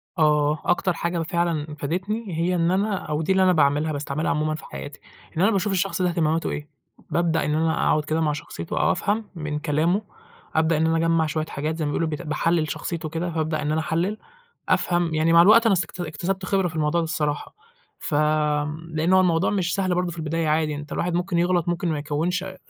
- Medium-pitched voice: Yes, medium, 165 Hz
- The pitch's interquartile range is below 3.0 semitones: Yes, narrow, 2.6 semitones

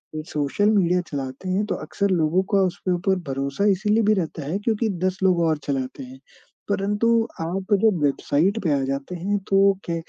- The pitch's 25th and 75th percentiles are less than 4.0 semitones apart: No, average, 4.7 semitones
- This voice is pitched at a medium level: Yes, medium, 180 Hz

